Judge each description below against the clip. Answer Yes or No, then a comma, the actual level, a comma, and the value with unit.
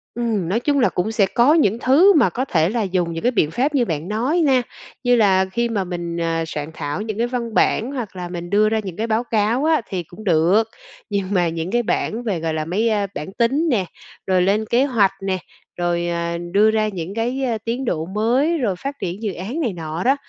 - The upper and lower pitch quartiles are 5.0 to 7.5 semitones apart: Yes, average, 5.3 semitones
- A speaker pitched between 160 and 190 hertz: No, high, 210 Hz